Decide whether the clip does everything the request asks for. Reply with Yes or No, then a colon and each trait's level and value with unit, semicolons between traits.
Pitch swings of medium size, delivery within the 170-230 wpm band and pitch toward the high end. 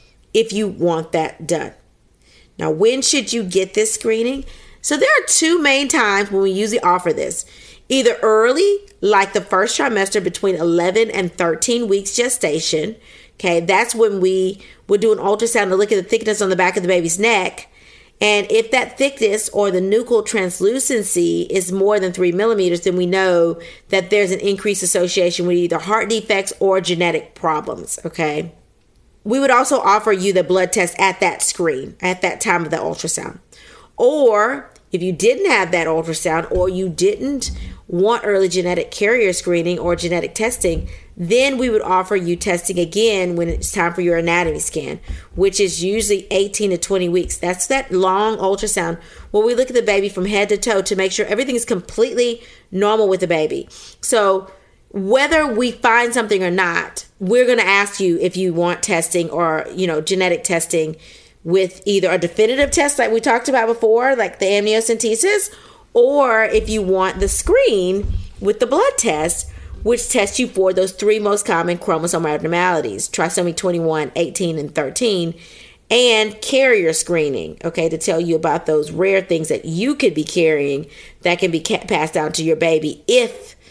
Yes: average, 4.3 semitones; average, 180 wpm; high, 195 Hz